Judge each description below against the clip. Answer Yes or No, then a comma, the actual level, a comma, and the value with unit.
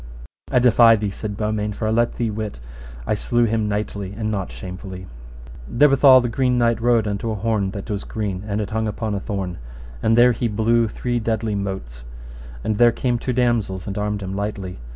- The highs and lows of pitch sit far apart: No, average, 2.7 semitones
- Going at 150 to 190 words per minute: No, average, 200 wpm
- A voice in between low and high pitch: No, low, 110 Hz